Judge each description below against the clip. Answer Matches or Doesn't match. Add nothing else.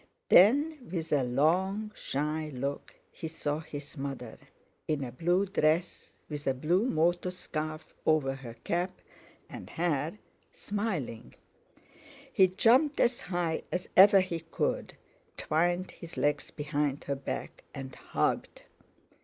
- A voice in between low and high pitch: Matches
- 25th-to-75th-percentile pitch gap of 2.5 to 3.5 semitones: Doesn't match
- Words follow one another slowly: Matches